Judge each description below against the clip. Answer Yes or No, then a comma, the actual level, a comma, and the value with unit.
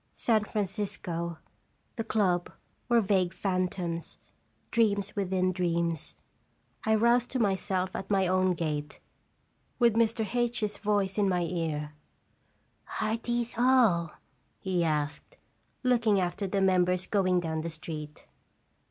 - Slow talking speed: Yes, slow, 125 wpm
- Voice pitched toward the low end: No, high, 190 Hz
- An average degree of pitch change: Yes, average, 4.0 semitones